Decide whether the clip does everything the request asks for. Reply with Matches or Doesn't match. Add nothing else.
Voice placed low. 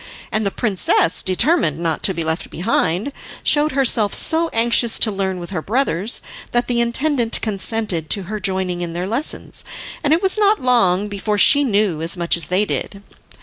Doesn't match